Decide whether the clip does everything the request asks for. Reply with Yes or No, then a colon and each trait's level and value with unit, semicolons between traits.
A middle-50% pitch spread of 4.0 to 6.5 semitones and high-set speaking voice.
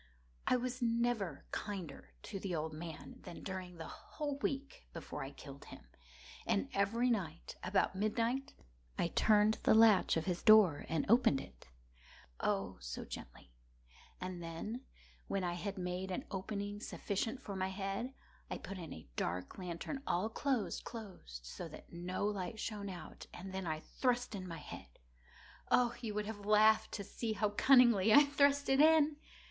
Yes: average, 4.9 semitones; high, 200 Hz